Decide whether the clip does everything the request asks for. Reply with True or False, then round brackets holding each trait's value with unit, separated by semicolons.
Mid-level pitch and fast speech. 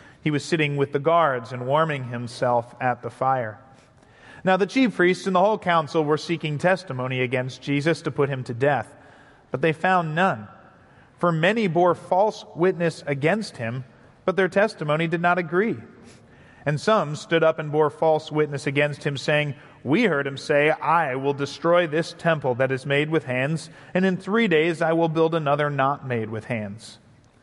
False (150 Hz; 185 wpm)